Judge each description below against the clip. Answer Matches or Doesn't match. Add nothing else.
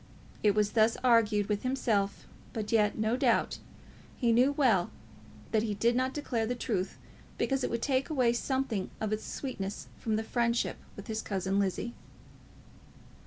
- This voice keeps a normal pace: Matches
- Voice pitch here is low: Doesn't match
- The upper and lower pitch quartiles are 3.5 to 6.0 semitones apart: Doesn't match